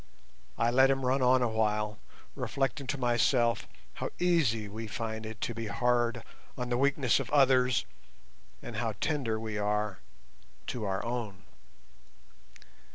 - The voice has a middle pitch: No, low, 120 Hz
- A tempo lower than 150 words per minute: Yes, average, 140 wpm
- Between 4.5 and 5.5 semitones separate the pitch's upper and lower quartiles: No, average, 3.0 semitones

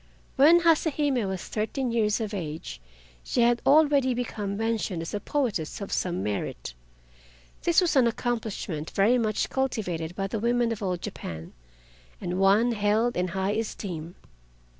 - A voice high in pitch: Yes, high, 215 Hz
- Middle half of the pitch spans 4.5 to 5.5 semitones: Yes, average, 4.8 semitones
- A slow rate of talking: No, average, 155 wpm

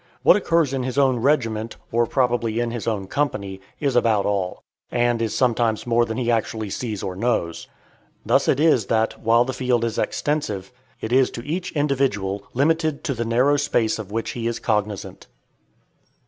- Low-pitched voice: Yes, low, 120 Hz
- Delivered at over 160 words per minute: Yes, average, 180 wpm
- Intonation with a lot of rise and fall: No, average, 3.3 semitones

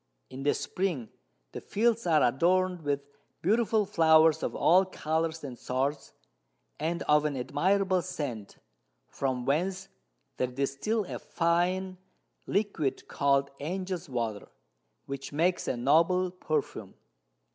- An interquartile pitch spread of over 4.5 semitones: Yes, average, 5.0 semitones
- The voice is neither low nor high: Yes, medium, 160 Hz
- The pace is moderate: No, slow, 120 wpm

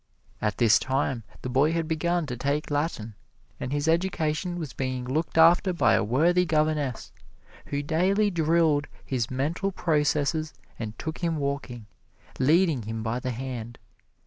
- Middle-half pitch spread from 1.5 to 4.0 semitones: No, average, 4.4 semitones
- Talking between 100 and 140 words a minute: No, average, 150 wpm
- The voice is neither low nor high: Yes, medium, 150 Hz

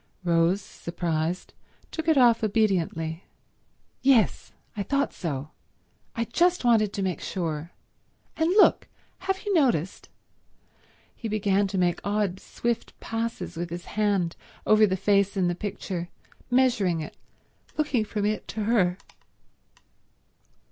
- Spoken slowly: Yes, slow, 120 wpm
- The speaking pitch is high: Yes, high, 205 Hz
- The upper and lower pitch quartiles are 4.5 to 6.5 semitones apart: Yes, average, 4.8 semitones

